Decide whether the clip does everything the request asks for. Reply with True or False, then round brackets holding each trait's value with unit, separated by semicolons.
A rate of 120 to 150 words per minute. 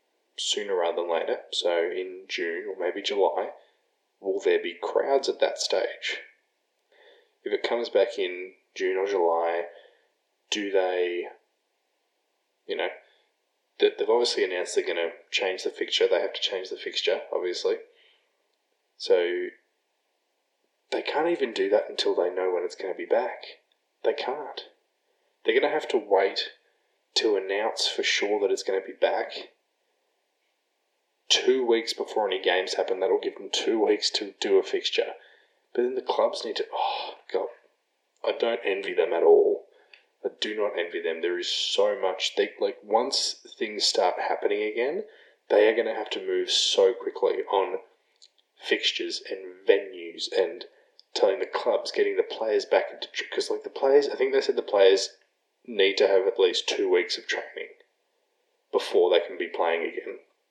False (170 wpm)